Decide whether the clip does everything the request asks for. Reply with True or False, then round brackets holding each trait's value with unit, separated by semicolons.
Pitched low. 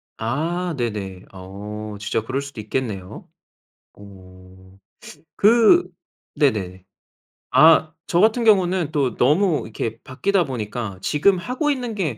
True (130 Hz)